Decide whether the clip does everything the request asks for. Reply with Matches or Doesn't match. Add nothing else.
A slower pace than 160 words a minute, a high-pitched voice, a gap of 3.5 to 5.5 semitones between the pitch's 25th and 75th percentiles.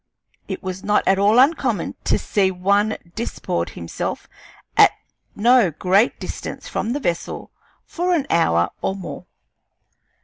Matches